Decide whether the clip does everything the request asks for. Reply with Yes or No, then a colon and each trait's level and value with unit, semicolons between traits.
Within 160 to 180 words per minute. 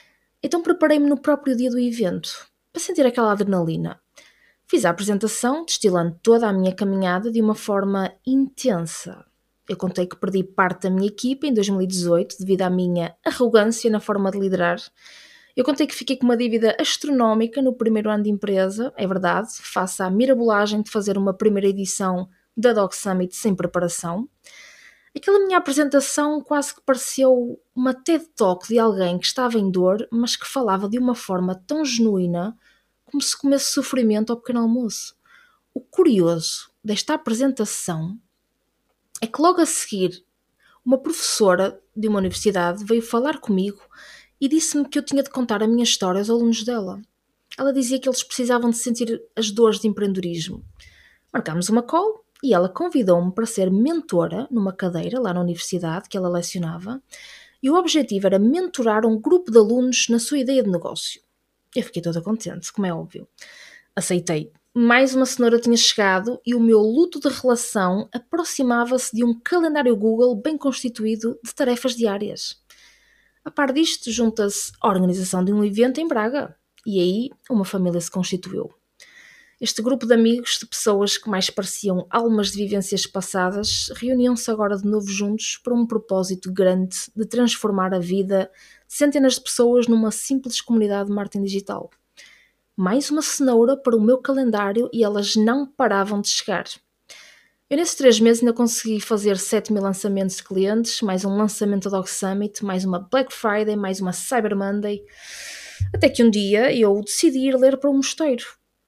Yes: average, 165 wpm